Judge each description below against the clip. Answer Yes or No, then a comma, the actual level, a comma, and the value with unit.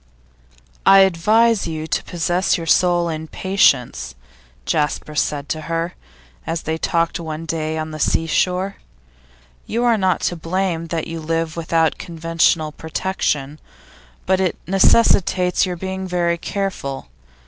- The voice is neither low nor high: Yes, medium, 165 Hz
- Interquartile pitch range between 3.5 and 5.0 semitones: No, average, 2.8 semitones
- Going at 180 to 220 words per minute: No, slow, 135 wpm